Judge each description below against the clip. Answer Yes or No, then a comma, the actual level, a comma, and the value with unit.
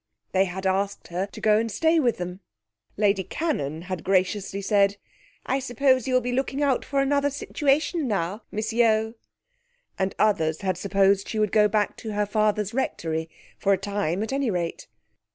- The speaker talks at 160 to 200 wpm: Yes, average, 180 wpm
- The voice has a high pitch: Yes, high, 210 Hz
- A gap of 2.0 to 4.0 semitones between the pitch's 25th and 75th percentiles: No, average, 4.5 semitones